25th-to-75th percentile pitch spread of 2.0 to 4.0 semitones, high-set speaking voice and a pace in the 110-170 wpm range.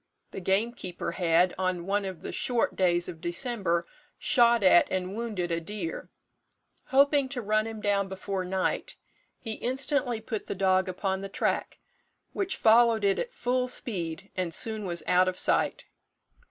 No: average, 4.4 semitones; high, 195 Hz; average, 160 wpm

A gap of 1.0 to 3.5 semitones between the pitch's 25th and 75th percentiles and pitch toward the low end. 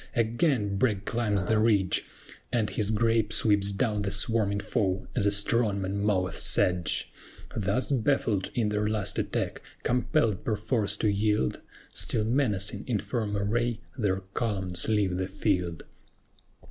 Yes: narrow, 2.4 semitones; low, 105 Hz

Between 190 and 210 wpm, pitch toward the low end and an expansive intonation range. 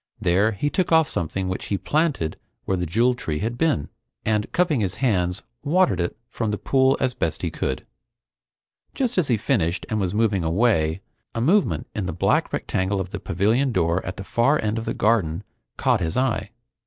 Yes: average, 195 wpm; low, 105 Hz; wide, 6.0 semitones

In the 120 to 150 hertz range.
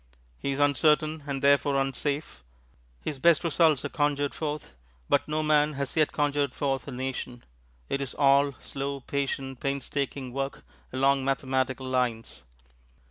Yes: medium, 140 Hz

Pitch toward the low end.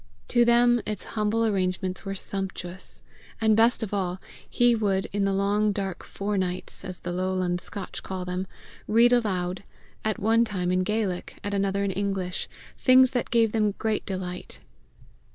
No: high, 200 Hz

